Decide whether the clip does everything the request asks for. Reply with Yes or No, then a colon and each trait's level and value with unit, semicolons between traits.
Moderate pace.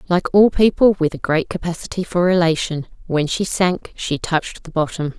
Yes: average, 185 wpm